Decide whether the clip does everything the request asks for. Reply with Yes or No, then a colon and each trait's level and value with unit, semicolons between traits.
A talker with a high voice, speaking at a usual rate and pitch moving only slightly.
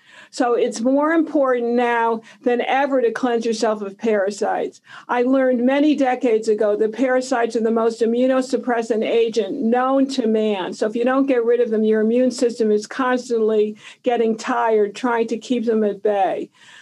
Yes: high, 235 Hz; average, 170 wpm; narrow, 2.2 semitones